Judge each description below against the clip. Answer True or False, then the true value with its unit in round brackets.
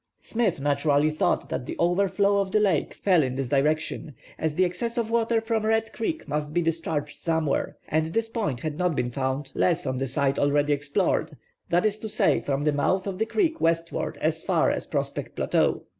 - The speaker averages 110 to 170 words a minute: False (205 wpm)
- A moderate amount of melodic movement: False (6.1 semitones)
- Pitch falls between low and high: True (165 Hz)